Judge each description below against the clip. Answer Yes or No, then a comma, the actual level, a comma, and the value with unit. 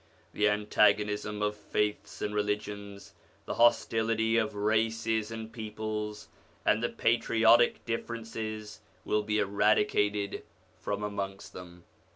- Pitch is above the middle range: No, low, 105 Hz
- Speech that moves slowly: Yes, slow, 110 wpm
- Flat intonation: Yes, narrow, 1.3 semitones